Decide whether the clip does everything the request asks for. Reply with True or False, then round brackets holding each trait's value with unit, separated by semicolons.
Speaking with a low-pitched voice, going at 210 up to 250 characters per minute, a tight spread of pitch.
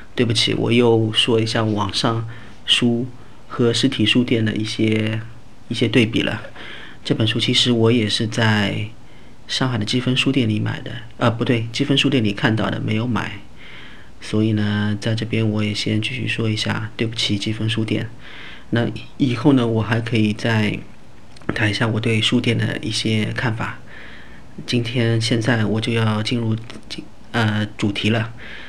True (115 Hz; 235 characters per minute; 1.8 semitones)